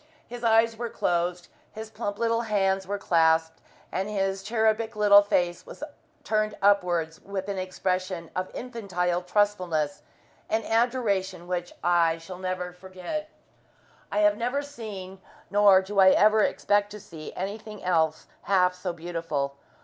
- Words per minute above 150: No, average, 140 wpm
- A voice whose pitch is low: No, high, 195 Hz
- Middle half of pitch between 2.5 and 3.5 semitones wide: Yes, average, 3.1 semitones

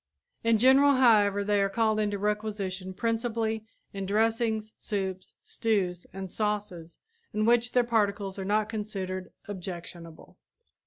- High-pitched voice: Yes, high, 210 Hz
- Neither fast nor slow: No, slow, 125 wpm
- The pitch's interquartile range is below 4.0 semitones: Yes, average, 2.7 semitones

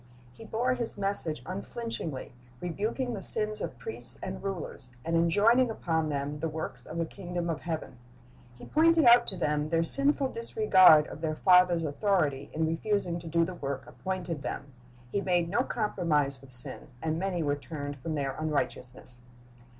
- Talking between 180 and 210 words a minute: No, average, 170 wpm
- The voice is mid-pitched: Yes, medium, 170 Hz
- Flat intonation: No, average, 5.2 semitones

